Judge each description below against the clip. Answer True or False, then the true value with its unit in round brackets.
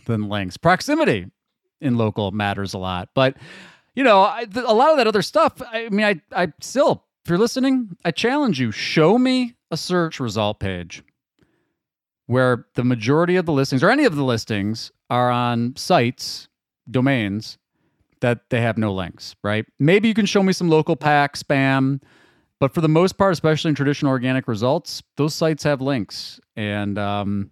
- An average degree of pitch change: False (7.7 semitones)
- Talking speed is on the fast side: False (180 wpm)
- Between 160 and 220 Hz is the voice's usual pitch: False (135 Hz)